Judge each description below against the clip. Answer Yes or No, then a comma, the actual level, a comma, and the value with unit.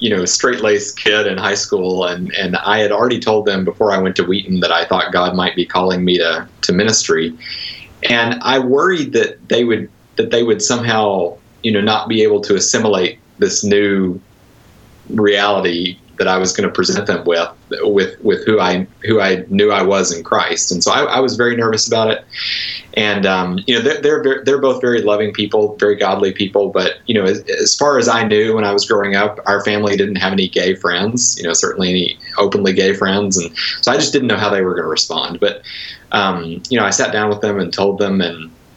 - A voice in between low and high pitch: No, low, 100 Hz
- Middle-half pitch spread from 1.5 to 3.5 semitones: No, average, 3.9 semitones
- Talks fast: Yes, fast, 225 wpm